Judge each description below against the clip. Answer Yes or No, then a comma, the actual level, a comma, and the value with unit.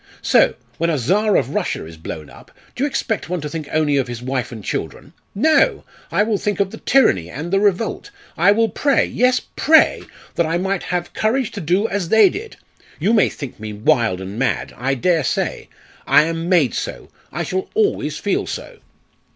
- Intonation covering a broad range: Yes, wide, 7.9 semitones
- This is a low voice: No, medium, 175 Hz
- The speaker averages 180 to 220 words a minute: Yes, average, 200 wpm